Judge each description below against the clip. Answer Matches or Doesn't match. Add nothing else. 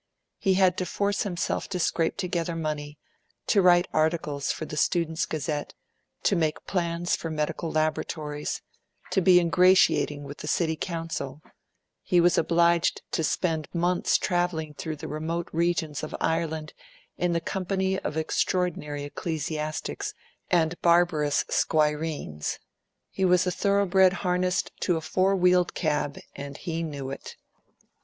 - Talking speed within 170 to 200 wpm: Doesn't match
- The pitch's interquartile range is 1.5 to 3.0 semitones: Matches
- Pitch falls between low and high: Matches